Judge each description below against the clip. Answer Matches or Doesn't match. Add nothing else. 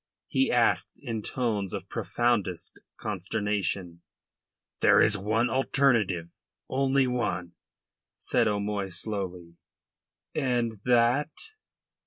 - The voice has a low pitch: Matches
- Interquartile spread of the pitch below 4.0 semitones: Doesn't match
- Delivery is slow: Matches